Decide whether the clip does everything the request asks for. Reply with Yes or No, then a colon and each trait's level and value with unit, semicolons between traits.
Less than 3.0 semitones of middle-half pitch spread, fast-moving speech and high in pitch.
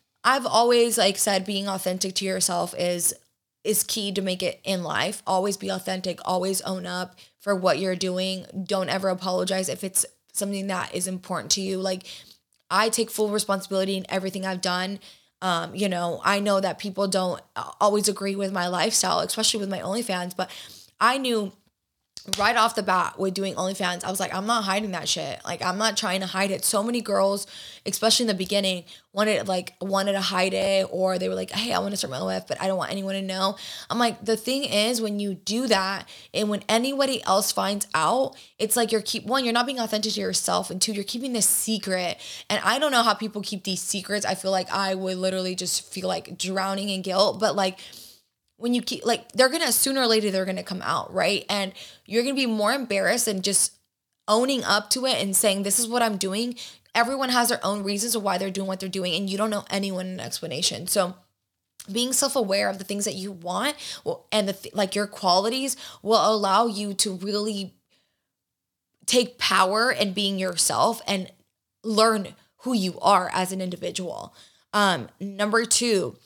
Yes: narrow, 2.5 semitones; fast, 210 wpm; high, 195 Hz